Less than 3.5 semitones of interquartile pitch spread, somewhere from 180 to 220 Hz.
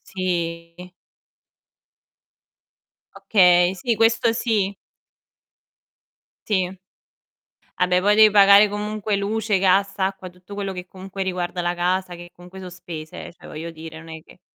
Yes: narrow, 2.4 semitones; medium, 185 Hz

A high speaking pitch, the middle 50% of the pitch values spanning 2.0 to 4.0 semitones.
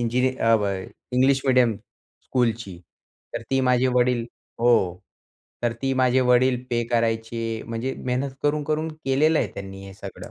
No: low, 125 Hz; narrow, 2.4 semitones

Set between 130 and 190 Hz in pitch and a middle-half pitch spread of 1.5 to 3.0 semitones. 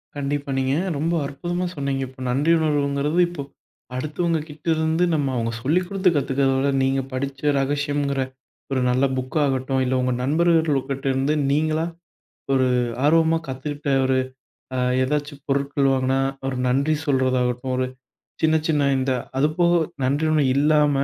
Yes: medium, 140 Hz; narrow, 2.6 semitones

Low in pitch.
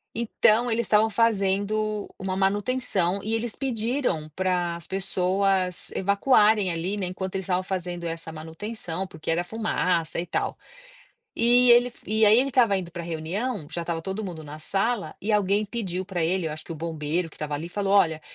No: high, 190 Hz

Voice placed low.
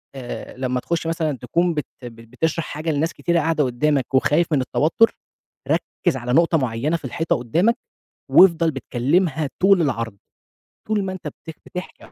No: medium, 155 Hz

